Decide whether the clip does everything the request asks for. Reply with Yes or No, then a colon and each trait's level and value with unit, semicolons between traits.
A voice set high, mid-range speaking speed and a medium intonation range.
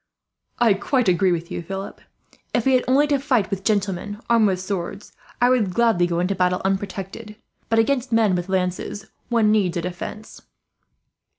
Yes: high, 200 Hz; average, 175 wpm; average, 3.9 semitones